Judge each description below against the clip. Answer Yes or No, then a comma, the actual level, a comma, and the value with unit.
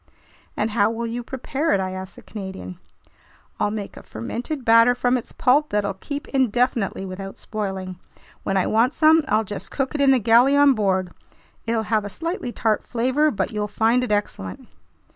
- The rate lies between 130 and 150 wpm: No, average, 180 wpm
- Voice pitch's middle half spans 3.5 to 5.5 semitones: Yes, average, 4.2 semitones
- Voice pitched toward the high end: Yes, high, 225 Hz